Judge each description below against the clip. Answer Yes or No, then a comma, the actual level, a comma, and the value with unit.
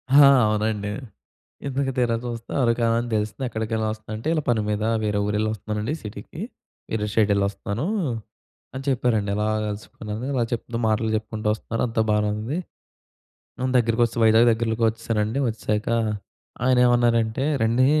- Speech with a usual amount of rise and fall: No, narrow, 1.9 semitones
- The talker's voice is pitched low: Yes, low, 110 Hz